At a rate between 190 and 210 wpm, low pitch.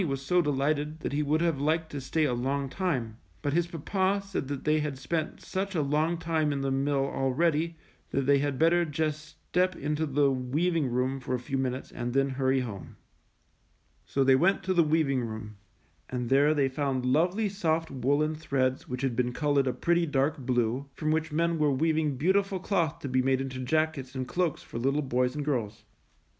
No: average, 200 wpm; medium, 145 Hz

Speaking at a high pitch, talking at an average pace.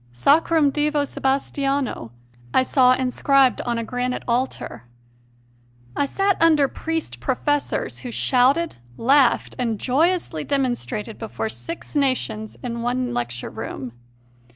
No: very high, 260 Hz; slow, 115 wpm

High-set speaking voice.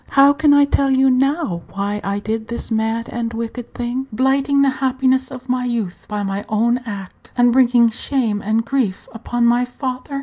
Yes: high, 245 Hz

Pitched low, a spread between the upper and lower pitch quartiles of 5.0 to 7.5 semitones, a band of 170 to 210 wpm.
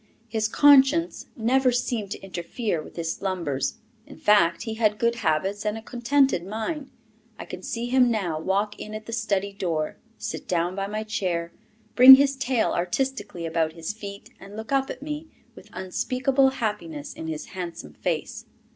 No: high, 210 Hz; wide, 5.6 semitones; average, 175 wpm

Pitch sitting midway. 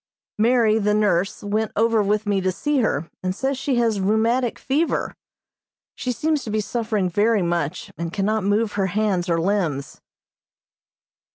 No: high, 210 Hz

